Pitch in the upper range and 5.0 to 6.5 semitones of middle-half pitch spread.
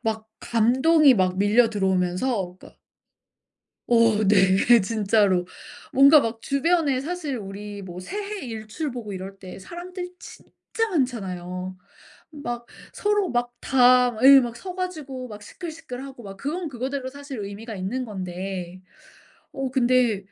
Yes: high, 240 Hz; wide, 5.8 semitones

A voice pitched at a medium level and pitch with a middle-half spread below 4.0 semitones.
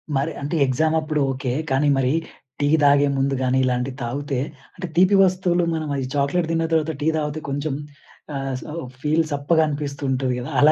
Yes: medium, 145 Hz; average, 2.9 semitones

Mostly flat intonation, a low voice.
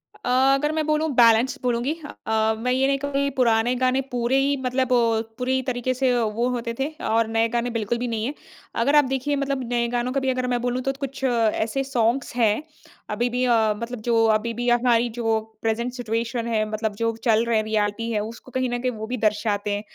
No: narrow, 2.3 semitones; high, 240 Hz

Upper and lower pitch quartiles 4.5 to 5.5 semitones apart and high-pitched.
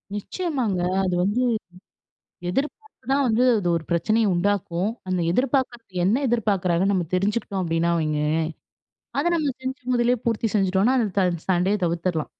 Yes: average, 5.2 semitones; high, 200 Hz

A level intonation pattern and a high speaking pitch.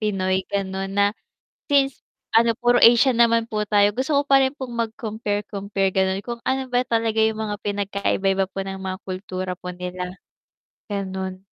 No: average, 3.4 semitones; high, 205 Hz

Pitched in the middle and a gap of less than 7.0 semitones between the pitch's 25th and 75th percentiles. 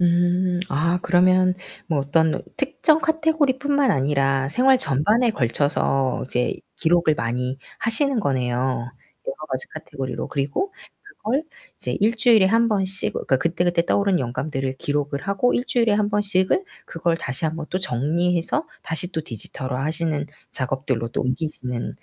No: medium, 170 Hz; wide, 7.6 semitones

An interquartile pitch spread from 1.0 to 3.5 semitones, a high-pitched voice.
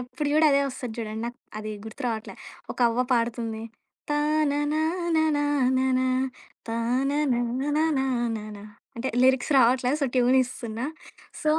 No: average, 3.9 semitones; very high, 255 Hz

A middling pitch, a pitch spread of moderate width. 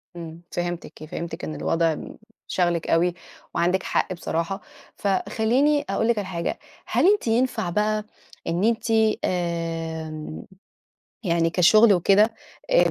Yes: medium, 175 Hz; average, 4.3 semitones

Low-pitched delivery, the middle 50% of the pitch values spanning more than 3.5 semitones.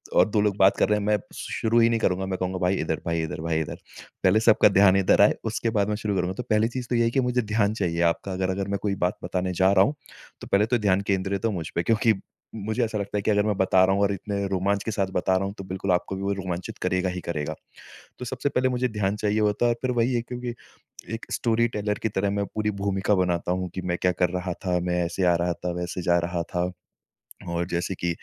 No: low, 100 Hz; average, 2.8 semitones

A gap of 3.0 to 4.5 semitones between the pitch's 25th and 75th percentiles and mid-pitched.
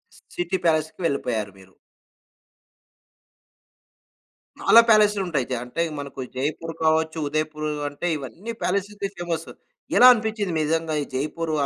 Yes: average, 4.2 semitones; medium, 160 Hz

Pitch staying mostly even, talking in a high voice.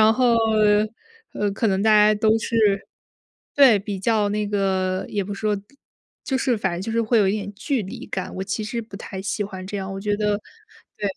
Yes: narrow, 2.0 semitones; high, 205 Hz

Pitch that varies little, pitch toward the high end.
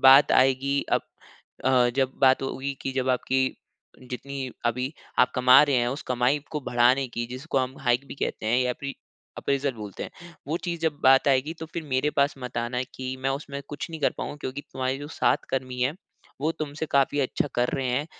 No: narrow, 1.8 semitones; low, 135 Hz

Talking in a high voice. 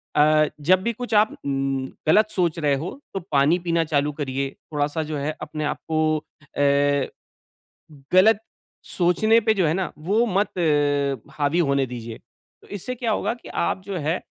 No: medium, 155 Hz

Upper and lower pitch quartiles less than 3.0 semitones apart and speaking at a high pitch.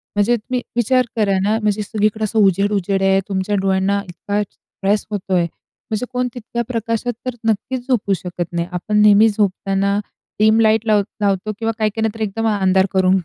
Yes: narrow, 2.4 semitones; high, 205 Hz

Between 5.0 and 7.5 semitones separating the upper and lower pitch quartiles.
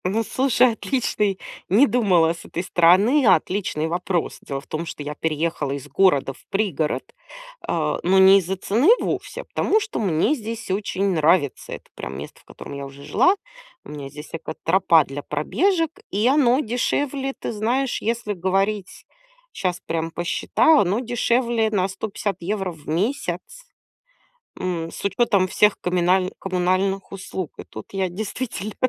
Yes: average, 5.3 semitones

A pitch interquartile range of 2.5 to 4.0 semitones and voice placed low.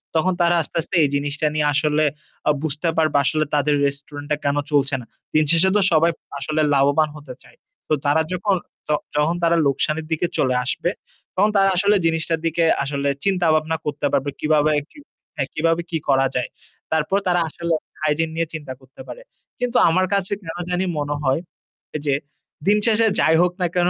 No: average, 2.9 semitones; medium, 155 Hz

